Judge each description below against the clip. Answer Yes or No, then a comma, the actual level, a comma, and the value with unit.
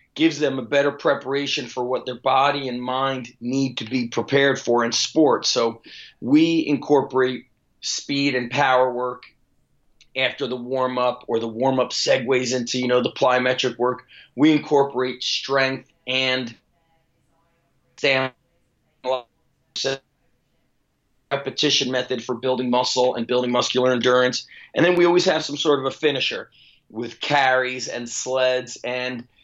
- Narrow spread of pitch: Yes, narrow, 1.8 semitones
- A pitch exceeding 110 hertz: Yes, low, 130 Hz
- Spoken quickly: No, average, 140 wpm